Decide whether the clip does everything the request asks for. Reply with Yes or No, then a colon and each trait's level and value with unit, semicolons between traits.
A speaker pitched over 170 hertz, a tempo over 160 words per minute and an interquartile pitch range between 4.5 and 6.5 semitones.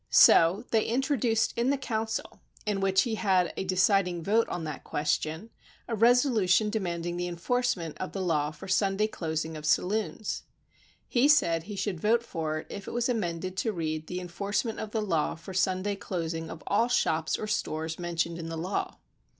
Yes: high, 190 Hz; average, 190 wpm; average, 4.8 semitones